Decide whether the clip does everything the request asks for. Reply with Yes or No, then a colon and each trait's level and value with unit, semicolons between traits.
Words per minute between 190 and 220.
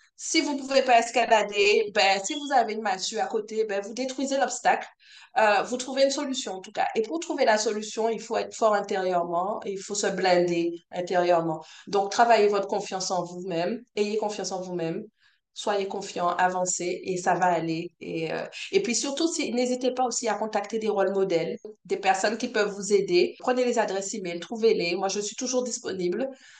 Yes: average, 200 wpm